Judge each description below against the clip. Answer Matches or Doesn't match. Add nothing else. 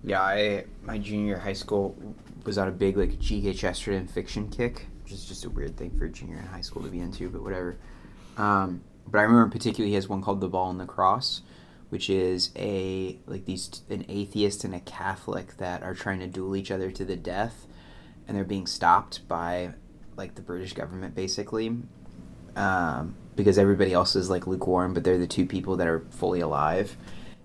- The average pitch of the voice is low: Matches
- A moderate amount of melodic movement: Doesn't match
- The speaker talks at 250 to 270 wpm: Doesn't match